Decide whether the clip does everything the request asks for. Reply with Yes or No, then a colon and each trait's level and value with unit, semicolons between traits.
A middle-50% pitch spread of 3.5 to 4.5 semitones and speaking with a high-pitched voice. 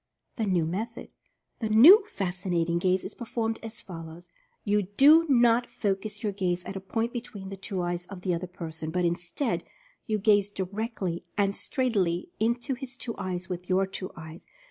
Yes: average, 4.2 semitones; high, 195 Hz